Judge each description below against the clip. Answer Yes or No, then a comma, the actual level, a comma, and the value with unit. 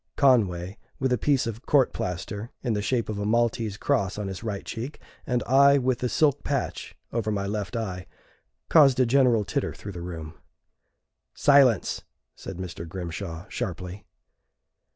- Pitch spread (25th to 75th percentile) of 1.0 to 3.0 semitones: No, average, 5.2 semitones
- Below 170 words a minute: Yes, average, 160 wpm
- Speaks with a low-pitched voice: Yes, low, 110 Hz